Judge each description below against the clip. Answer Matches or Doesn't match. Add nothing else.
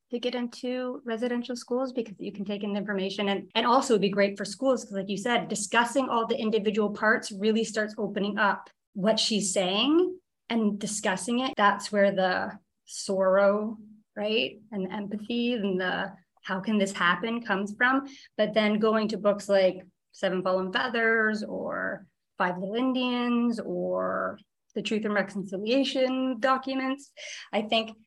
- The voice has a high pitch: Matches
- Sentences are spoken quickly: Doesn't match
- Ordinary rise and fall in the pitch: Matches